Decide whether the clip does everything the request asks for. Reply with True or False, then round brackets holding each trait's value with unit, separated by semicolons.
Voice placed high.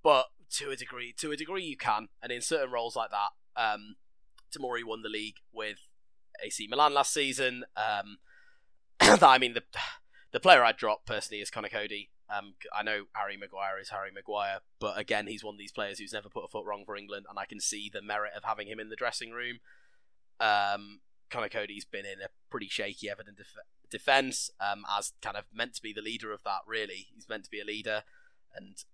False (110 Hz)